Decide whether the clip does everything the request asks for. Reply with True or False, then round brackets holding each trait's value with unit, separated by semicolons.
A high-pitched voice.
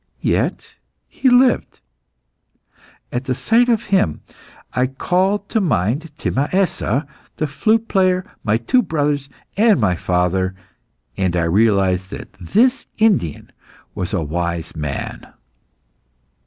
False (135 Hz)